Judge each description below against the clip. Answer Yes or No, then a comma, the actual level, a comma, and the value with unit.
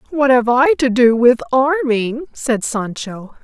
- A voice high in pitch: Yes, very high, 250 Hz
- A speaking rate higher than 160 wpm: No, average, 155 wpm